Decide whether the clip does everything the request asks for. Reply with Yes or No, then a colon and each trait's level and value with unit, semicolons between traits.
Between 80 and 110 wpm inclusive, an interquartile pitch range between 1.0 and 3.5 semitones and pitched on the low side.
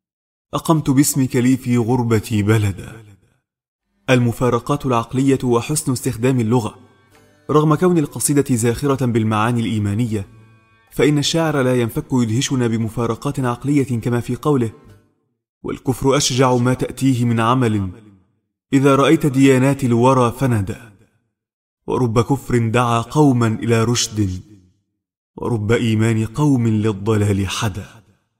Yes: average, 105 wpm; average, 3.0 semitones; low, 120 Hz